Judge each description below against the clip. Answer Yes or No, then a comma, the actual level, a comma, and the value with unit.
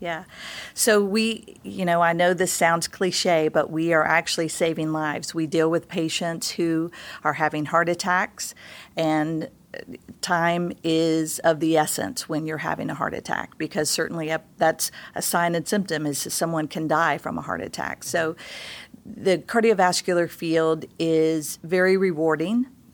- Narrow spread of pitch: Yes, narrow, 2.2 semitones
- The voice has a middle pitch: Yes, medium, 165 Hz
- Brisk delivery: No, average, 160 wpm